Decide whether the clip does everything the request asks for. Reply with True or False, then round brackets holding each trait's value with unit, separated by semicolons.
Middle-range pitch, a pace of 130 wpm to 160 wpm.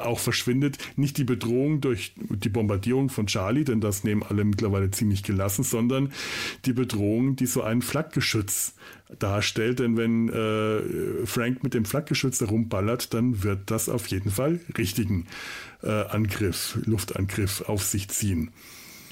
False (115 Hz; 145 wpm)